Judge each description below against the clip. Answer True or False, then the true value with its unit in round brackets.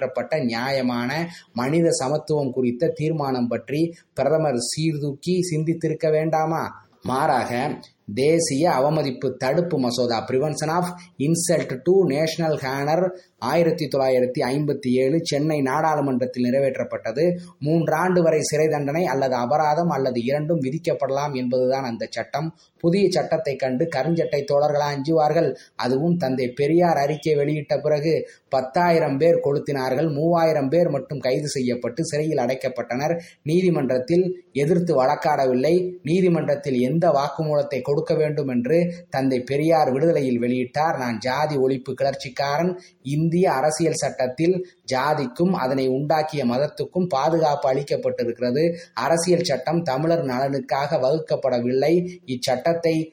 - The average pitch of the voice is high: False (150 Hz)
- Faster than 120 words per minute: False (105 wpm)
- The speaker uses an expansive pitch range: False (4.0 semitones)